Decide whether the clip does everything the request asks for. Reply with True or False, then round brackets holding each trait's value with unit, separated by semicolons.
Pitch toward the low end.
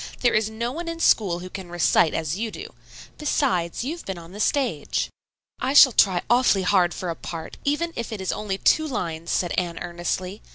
False (195 Hz)